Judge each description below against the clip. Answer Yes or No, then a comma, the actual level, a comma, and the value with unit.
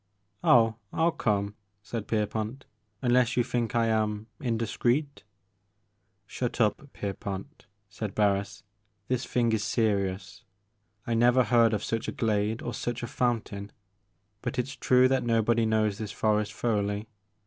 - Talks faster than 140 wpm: Yes, average, 150 wpm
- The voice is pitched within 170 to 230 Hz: No, low, 110 Hz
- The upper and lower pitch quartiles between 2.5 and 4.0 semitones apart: Yes, average, 2.8 semitones